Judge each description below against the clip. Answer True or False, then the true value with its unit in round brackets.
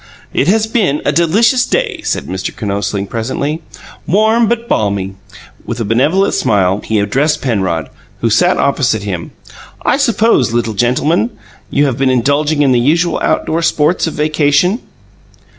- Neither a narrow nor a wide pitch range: False (8.3 semitones)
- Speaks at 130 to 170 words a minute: True (150 wpm)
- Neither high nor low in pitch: True (145 Hz)